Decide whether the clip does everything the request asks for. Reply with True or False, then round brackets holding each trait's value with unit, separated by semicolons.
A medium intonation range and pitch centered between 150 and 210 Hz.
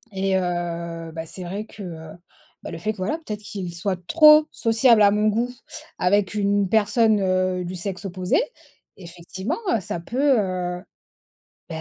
True (3.1 semitones; 190 Hz)